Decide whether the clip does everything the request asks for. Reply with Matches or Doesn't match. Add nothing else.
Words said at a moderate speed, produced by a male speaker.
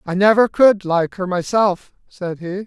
Matches